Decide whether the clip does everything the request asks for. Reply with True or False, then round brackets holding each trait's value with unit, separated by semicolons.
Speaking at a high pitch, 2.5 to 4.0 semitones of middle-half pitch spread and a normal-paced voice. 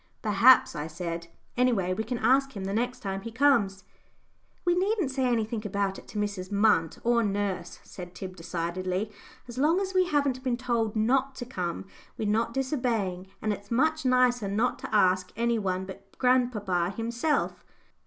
False (220 Hz; 4.7 semitones; 175 wpm)